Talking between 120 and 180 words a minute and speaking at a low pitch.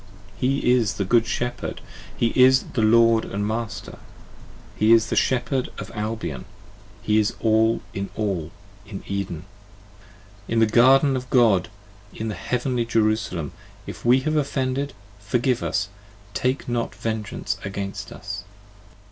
Yes: average, 140 wpm; low, 115 Hz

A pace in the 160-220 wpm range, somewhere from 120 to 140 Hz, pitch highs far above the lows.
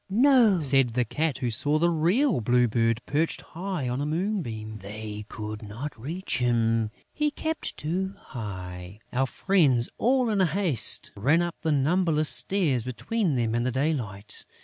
Yes: average, 165 wpm; low, 135 Hz; wide, 7.6 semitones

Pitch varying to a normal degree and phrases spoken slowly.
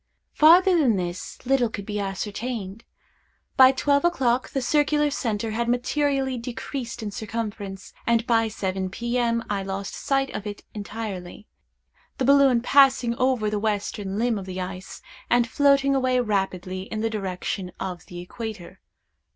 No: average, 4.7 semitones; average, 150 wpm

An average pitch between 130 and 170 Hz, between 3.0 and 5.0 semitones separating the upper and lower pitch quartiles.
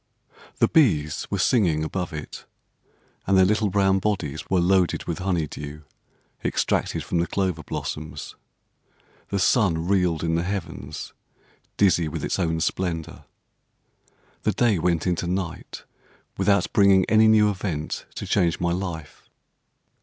No: very low, 90 Hz; average, 3.3 semitones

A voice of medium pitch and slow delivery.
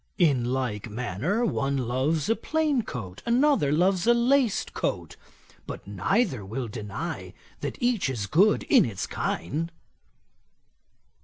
Yes: medium, 145 Hz; slow, 130 wpm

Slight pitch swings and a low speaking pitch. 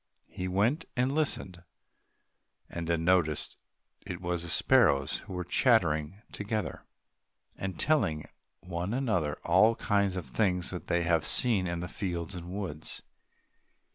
No: average, 3.6 semitones; very low, 90 Hz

